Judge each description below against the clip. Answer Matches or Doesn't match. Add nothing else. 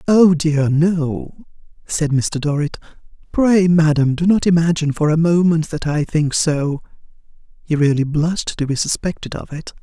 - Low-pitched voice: Doesn't match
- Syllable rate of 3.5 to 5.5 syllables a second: Matches